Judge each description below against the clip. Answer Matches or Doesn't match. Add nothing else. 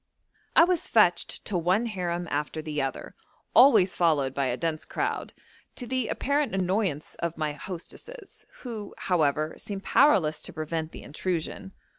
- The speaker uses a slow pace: Doesn't match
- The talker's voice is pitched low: Doesn't match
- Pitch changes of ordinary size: Doesn't match